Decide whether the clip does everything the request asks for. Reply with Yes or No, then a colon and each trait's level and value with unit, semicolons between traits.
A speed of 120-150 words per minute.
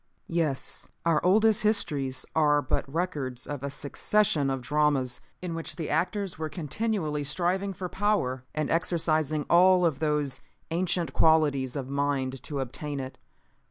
Yes: average, 145 wpm